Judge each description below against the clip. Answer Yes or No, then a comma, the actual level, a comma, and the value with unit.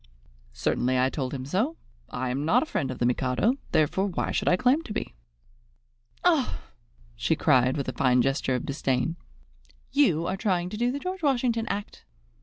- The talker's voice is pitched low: No, medium, 165 Hz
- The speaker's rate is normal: Yes, average, 185 wpm